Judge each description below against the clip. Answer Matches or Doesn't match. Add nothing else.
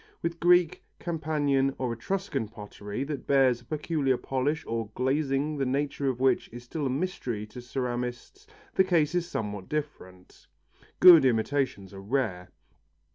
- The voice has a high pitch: Doesn't match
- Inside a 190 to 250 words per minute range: Doesn't match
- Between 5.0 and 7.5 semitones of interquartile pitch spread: Doesn't match